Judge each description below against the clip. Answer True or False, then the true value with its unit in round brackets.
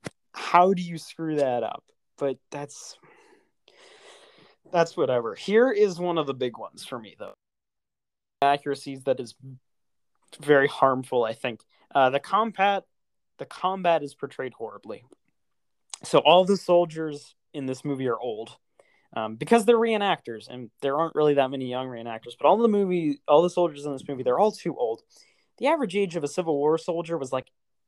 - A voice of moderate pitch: True (155 Hz)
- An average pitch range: False (6.0 semitones)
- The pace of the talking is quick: False (170 wpm)